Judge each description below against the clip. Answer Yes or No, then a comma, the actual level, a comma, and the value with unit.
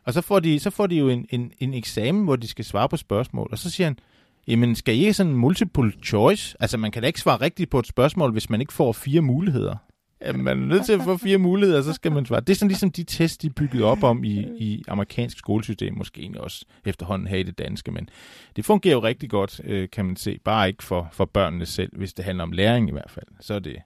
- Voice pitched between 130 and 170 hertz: No, low, 120 Hz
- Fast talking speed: Yes, fast, 270 wpm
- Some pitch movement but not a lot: No, wide, 8.2 semitones